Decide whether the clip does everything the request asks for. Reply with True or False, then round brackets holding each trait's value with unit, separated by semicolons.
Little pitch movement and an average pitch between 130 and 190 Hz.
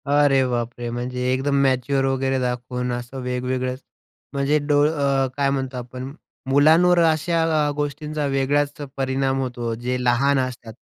True (2.1 semitones; 135 Hz)